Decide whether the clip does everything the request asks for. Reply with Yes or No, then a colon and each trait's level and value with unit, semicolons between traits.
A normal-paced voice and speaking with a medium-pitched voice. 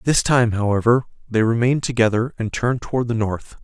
No: average, 180 wpm; low, 115 Hz